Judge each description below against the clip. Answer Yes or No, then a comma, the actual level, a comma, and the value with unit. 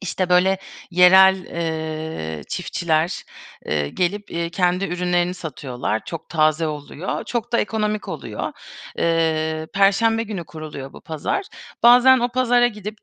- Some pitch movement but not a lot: Yes, average, 4.7 semitones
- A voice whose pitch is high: No, medium, 180 Hz